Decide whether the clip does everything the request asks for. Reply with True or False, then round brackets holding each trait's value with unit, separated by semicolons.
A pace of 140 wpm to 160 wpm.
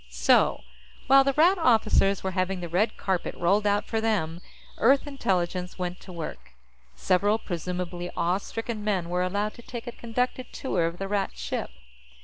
False (170 wpm)